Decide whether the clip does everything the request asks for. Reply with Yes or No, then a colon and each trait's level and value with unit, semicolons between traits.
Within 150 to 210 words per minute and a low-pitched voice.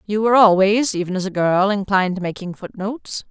No: average, 200 wpm; high, 200 Hz